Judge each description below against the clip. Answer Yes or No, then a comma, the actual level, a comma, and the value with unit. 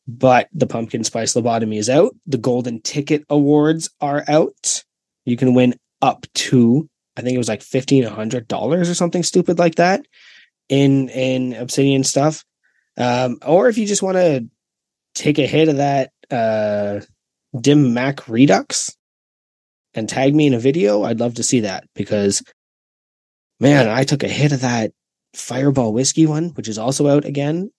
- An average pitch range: Yes, average, 3.6 semitones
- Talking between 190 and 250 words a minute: No, average, 170 wpm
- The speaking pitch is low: Yes, low, 130 Hz